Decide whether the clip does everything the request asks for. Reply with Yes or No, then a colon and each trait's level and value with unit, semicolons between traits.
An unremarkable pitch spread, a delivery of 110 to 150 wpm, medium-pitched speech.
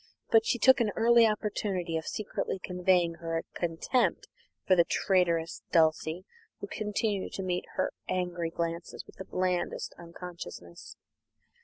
Yes: average, 3.5 semitones; slow, 135 wpm; medium, 180 Hz